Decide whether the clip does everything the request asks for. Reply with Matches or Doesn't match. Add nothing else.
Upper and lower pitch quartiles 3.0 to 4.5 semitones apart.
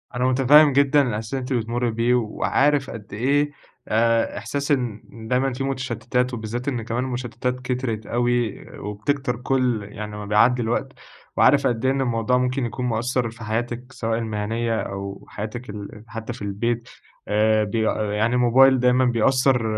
Doesn't match